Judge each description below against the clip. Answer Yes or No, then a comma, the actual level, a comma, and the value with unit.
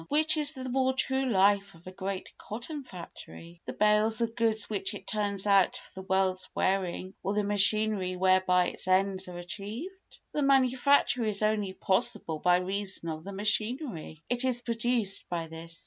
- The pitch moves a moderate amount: Yes, average, 4.1 semitones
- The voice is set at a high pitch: Yes, high, 200 Hz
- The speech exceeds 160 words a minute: Yes, average, 170 wpm